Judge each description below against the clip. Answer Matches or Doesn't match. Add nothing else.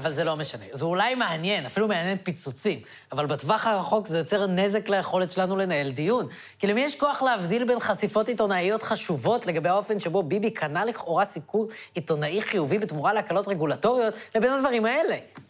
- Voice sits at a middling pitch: Doesn't match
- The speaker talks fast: Matches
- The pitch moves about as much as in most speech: Matches